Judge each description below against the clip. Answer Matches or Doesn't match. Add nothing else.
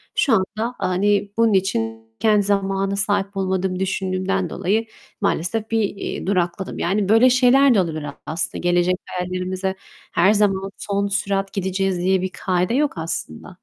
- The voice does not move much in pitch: Matches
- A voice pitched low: Doesn't match